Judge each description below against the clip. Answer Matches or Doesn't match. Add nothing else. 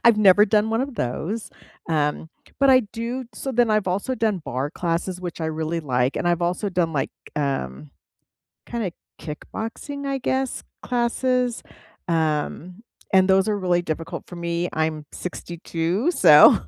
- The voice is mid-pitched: Matches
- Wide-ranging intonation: Matches